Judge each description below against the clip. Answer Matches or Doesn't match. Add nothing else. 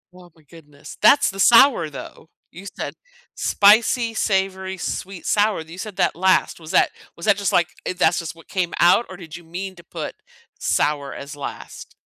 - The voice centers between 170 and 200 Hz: Matches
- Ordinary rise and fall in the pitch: Matches